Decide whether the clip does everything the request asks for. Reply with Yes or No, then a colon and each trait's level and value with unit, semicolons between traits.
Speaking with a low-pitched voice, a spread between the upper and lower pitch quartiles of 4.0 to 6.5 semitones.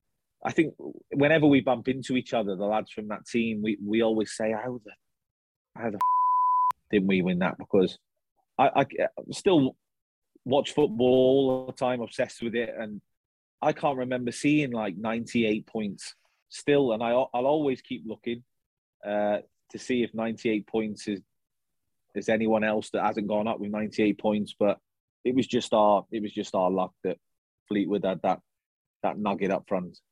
No: low, 110 Hz; average, 3.4 semitones